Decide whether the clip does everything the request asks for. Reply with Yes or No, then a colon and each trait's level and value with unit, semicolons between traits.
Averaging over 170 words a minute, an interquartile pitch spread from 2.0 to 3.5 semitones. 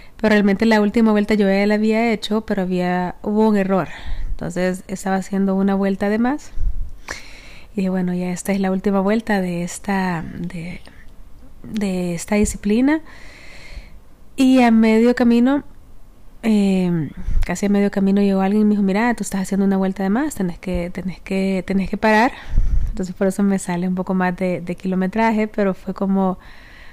Yes: average, 180 wpm; narrow, 2.4 semitones